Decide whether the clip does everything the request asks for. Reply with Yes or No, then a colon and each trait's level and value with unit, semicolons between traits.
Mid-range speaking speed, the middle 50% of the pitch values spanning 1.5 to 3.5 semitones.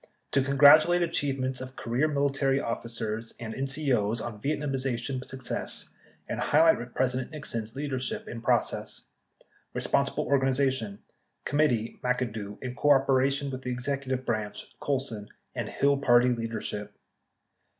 No: slow, 130 wpm; average, 3.0 semitones